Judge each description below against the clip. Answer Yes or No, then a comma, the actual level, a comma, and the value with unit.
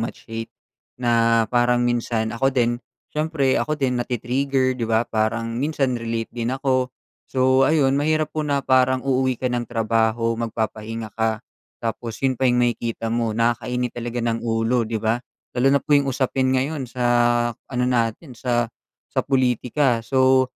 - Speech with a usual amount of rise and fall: No, narrow, 2.3 semitones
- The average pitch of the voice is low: Yes, low, 120 Hz